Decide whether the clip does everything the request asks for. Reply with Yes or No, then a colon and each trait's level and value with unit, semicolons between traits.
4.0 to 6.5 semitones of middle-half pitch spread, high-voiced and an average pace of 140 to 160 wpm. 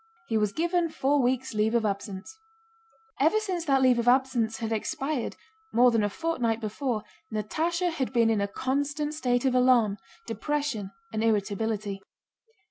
Yes: average, 5.0 semitones; high, 245 Hz; average, 155 wpm